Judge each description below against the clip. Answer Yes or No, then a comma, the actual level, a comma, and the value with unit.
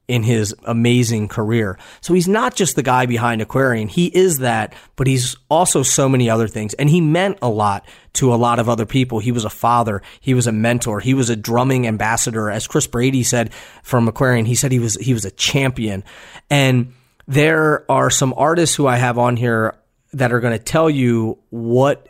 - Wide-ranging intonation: No, average, 2.8 semitones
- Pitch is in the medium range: No, low, 120 Hz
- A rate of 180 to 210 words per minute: Yes, fast, 205 wpm